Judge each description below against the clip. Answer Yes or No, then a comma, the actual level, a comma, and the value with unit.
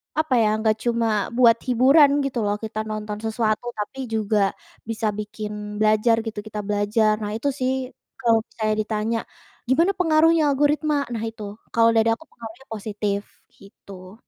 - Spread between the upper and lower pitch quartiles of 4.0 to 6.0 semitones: No, average, 3.1 semitones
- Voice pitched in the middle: No, high, 225 Hz